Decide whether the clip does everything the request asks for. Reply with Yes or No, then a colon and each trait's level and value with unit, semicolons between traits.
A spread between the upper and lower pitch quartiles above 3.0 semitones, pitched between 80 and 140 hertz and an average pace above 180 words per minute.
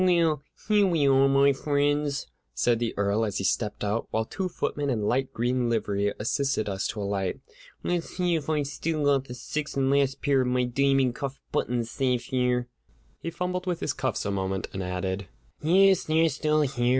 Yes: average, 4.8 semitones; low, 135 Hz; average, 195 wpm